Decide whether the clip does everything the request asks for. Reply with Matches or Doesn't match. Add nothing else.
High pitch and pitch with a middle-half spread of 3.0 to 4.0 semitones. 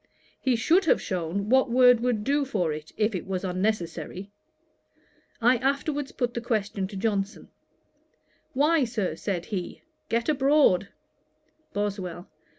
Doesn't match